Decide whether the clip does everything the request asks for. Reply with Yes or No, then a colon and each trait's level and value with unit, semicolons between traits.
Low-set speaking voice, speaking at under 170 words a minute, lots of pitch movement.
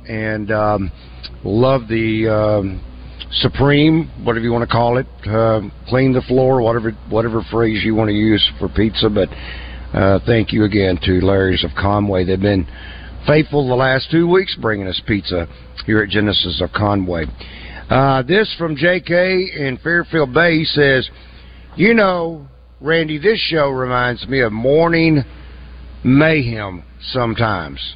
Yes: low, 110 Hz; average, 150 wpm; wide, 6.5 semitones